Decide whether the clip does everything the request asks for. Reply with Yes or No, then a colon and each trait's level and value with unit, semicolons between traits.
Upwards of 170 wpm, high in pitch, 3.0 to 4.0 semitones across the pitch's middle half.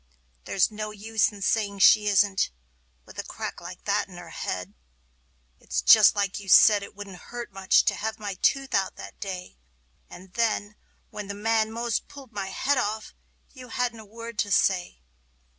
No: average, 180 wpm; high, 205 Hz; narrow, 2.6 semitones